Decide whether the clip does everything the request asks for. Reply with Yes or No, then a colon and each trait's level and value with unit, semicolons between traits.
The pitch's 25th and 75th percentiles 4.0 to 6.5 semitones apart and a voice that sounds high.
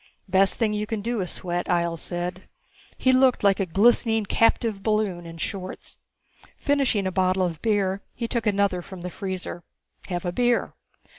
No: average, 3.6 semitones; high, 195 Hz